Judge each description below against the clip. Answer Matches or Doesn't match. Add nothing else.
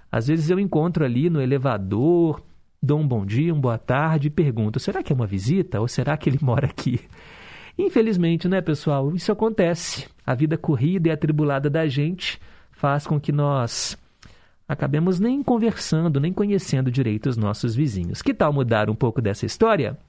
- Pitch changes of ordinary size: Matches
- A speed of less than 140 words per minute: Doesn't match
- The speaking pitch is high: Doesn't match